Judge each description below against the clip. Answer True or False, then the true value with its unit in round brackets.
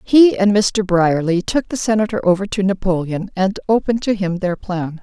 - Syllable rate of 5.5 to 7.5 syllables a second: False (5.0 syllables/s)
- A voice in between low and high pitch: False (195 Hz)